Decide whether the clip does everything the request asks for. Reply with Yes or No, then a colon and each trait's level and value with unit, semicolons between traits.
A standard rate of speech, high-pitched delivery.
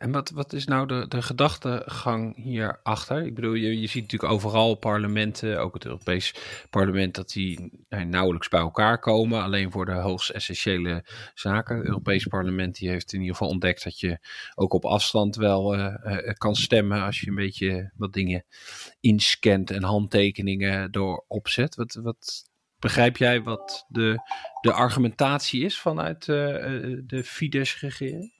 No: average, 165 wpm; low, 110 Hz